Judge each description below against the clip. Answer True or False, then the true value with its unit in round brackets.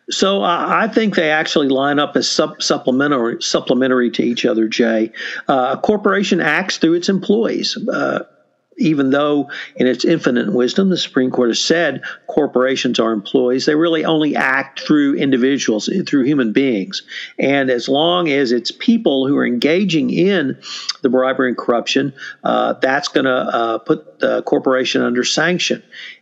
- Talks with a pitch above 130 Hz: True (140 Hz)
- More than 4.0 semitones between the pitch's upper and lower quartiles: True (4.8 semitones)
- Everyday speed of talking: True (160 wpm)